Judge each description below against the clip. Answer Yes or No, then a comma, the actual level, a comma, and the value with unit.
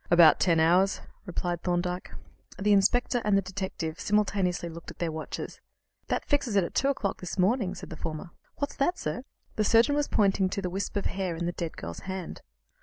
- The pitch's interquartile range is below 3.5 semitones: Yes, average, 3.1 semitones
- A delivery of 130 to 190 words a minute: No, average, 200 wpm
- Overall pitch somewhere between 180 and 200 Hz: Yes, high, 190 Hz